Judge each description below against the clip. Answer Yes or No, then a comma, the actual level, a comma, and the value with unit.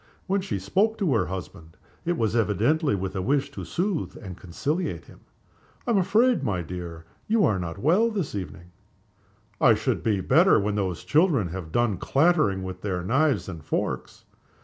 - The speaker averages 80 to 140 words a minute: No, average, 175 wpm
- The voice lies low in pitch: Yes, low, 110 Hz